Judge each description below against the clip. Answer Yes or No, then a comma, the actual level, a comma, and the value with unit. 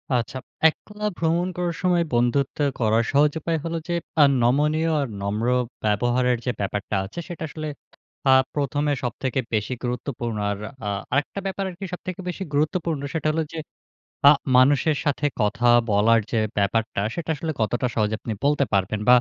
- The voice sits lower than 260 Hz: Yes, medium, 140 Hz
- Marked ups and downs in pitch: Yes, wide, 5.9 semitones